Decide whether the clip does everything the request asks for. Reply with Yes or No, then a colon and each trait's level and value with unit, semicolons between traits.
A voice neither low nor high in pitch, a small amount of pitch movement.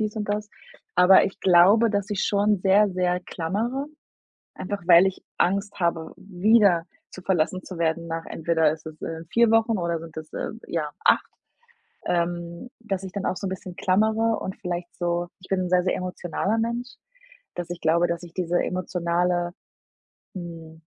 No: medium, 180 Hz; average, 3.0 semitones